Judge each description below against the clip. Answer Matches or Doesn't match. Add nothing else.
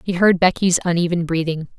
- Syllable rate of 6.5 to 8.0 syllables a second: Doesn't match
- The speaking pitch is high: Doesn't match